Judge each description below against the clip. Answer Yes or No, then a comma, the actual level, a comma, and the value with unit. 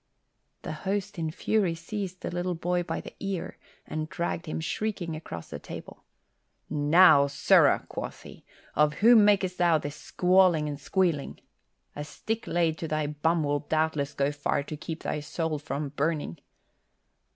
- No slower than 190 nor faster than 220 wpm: No, average, 160 wpm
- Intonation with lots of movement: No, average, 3.4 semitones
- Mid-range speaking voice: Yes, medium, 160 Hz